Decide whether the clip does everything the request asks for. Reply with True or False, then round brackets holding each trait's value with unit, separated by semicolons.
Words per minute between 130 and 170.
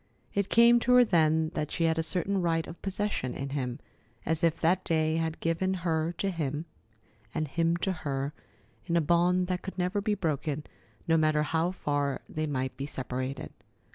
False (190 wpm)